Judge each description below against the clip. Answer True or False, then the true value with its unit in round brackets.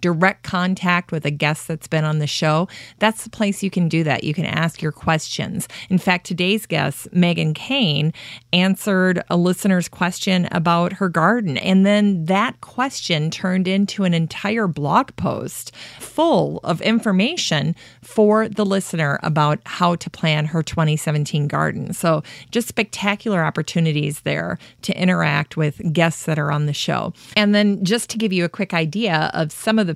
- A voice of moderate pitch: True (175 Hz)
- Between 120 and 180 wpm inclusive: True (170 wpm)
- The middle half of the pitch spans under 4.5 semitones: True (4.0 semitones)